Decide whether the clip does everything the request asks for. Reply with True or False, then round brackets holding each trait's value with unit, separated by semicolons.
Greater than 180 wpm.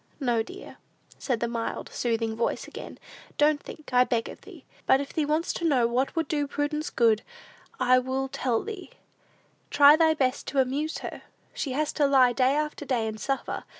True (190 wpm)